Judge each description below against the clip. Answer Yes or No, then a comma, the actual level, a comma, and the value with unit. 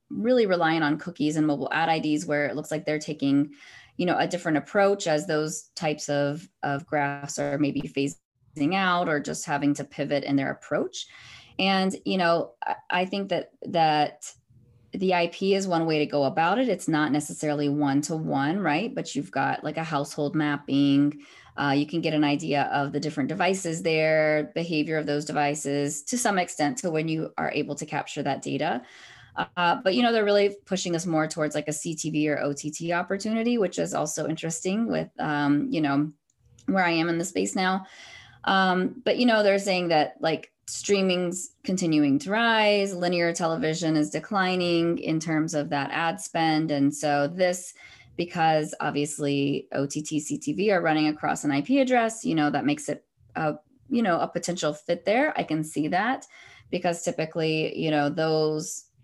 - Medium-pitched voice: Yes, medium, 155 Hz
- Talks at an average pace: Yes, average, 185 wpm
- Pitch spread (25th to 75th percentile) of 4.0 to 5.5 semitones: No, average, 3.5 semitones